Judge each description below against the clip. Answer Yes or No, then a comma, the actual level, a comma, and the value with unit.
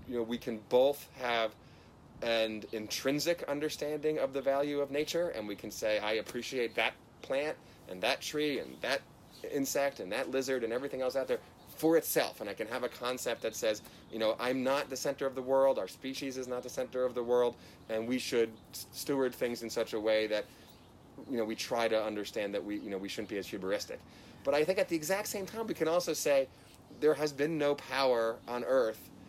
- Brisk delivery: Yes, fast, 220 wpm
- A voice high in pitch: No, low, 130 Hz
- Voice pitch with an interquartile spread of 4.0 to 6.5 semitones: Yes, average, 4.4 semitones